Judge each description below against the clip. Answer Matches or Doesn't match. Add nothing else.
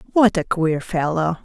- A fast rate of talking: Doesn't match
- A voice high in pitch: Doesn't match